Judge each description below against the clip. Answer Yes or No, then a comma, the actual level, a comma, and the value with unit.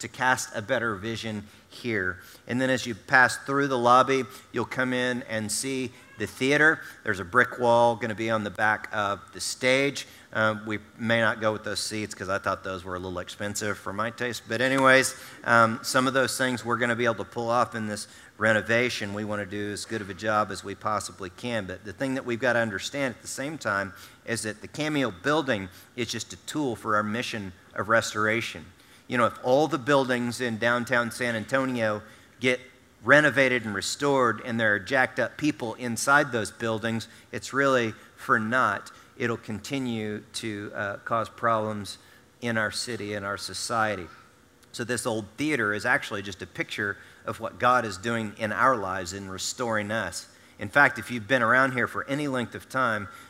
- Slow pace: No, fast, 205 wpm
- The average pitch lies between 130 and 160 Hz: No, low, 115 Hz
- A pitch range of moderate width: Yes, average, 3.2 semitones